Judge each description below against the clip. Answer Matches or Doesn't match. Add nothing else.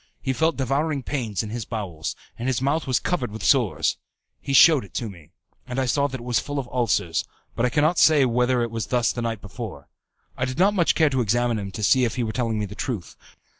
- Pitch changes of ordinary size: Matches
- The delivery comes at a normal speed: Doesn't match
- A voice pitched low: Matches